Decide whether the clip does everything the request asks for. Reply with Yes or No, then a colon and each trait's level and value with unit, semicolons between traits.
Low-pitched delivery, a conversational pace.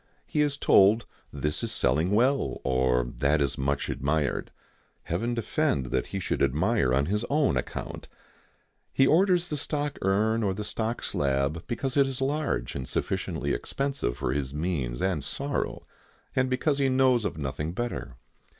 Yes: very low, 95 Hz; average, 160 wpm